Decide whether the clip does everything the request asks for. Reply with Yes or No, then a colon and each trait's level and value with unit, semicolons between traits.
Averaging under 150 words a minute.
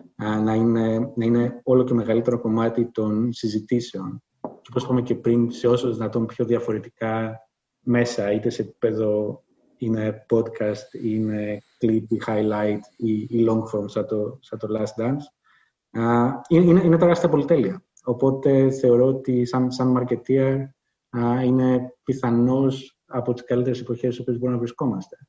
Yes: average, 140 wpm